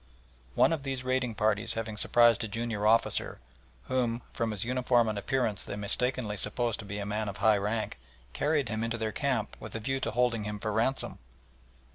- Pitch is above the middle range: No, low, 115 Hz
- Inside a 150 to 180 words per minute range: No, average, 195 wpm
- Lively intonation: No, average, 2.8 semitones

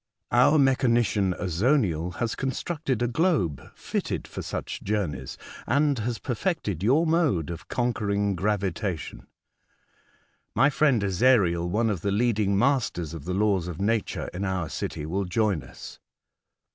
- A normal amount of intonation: No, wide, 5.8 semitones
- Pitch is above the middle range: No, low, 105 Hz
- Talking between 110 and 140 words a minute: Yes, slow, 135 wpm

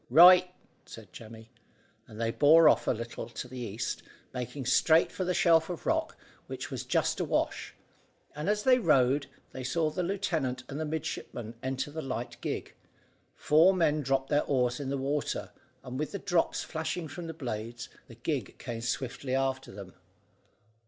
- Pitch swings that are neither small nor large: Yes, average, 4.6 semitones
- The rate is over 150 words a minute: Yes, average, 170 wpm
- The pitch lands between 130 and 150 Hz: Yes, low, 135 Hz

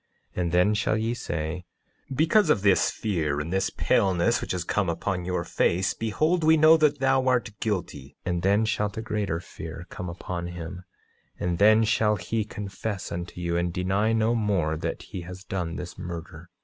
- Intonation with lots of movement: No, average, 4.2 semitones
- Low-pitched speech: Yes, very low, 95 Hz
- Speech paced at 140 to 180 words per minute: No, average, 190 wpm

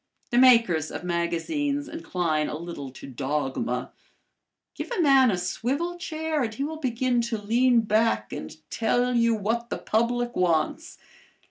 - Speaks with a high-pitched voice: Yes, high, 230 Hz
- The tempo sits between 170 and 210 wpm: No, average, 150 wpm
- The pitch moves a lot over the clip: Yes, wide, 7.6 semitones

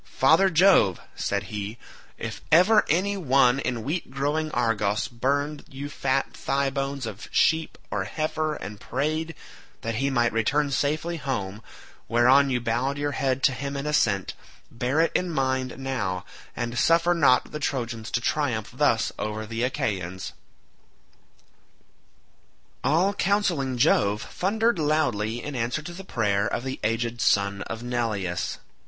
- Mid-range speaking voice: No, low, 130 Hz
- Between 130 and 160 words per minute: Yes, average, 145 wpm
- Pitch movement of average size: Yes, average, 4.9 semitones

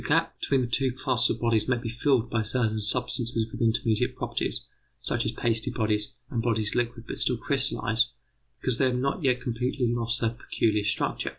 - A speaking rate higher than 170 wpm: Yes, average, 195 wpm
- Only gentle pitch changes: Yes, narrow, 2.0 semitones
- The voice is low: Yes, low, 120 Hz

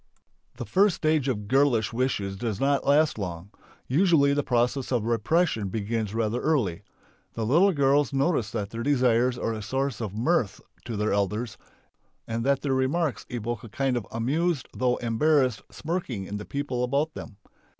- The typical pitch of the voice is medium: No, low, 125 Hz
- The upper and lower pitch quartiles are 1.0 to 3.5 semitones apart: No, average, 4.4 semitones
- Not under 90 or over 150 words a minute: No, average, 170 wpm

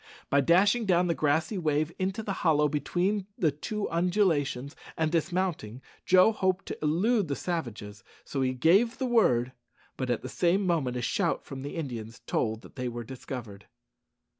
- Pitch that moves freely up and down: Yes, wide, 6.3 semitones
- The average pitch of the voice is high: No, medium, 160 Hz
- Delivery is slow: No, average, 170 wpm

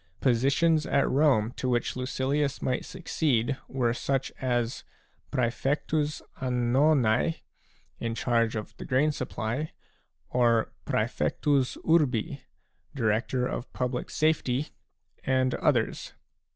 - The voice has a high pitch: No, low, 130 Hz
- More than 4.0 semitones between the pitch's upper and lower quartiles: No, average, 3.1 semitones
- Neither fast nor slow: No, slow, 100 wpm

